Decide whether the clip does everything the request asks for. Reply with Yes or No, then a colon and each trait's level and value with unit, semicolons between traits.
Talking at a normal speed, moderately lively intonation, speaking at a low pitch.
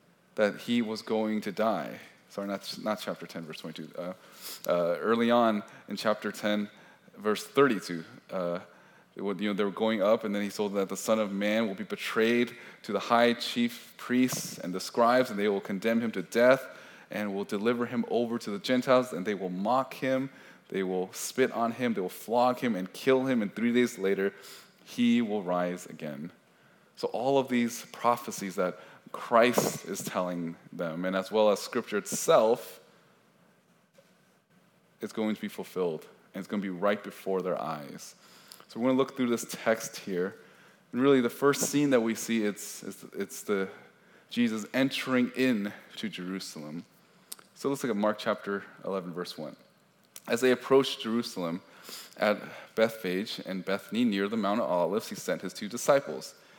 Yes: average, 185 wpm; average, 3.7 semitones; low, 110 Hz